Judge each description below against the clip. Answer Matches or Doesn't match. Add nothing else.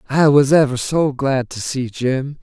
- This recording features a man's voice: Matches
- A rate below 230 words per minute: Matches